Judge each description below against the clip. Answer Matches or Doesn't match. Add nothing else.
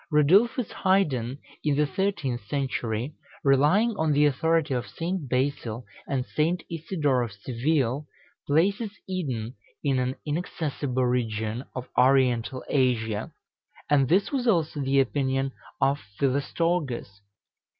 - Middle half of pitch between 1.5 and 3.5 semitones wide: Doesn't match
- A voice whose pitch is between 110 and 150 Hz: Matches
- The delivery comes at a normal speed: Doesn't match